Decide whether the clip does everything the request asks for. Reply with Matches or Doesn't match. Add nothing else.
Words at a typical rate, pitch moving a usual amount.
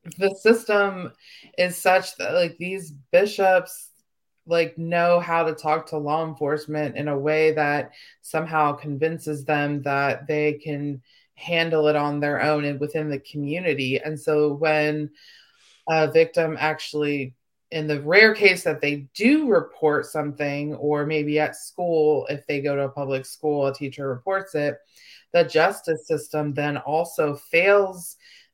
Doesn't match